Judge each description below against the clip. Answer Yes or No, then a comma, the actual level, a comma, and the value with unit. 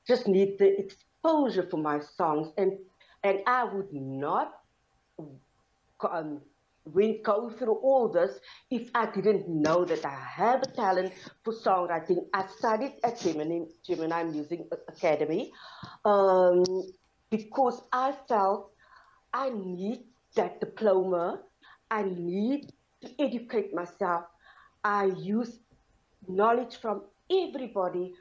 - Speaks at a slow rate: Yes, slow, 110 wpm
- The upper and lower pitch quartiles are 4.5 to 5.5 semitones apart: Yes, average, 4.8 semitones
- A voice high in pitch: Yes, high, 195 Hz